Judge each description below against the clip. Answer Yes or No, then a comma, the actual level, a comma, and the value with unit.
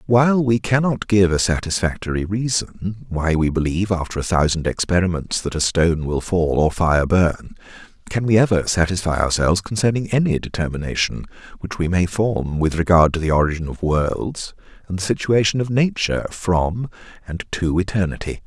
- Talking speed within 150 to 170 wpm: Yes, average, 165 wpm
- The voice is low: Yes, very low, 90 Hz